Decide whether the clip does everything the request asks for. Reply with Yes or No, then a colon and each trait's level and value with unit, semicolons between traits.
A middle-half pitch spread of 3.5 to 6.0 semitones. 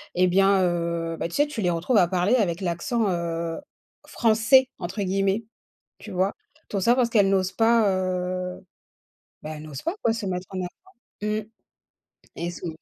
Yes: average, 3.8 semitones